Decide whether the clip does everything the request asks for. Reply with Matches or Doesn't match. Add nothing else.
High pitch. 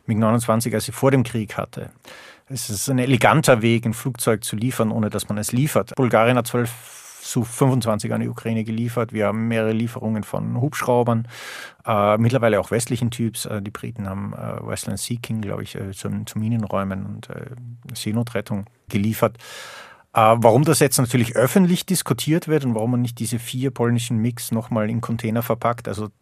Doesn't match